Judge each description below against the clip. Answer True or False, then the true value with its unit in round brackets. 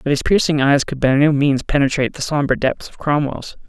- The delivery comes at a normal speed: False (230 wpm)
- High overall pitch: False (140 Hz)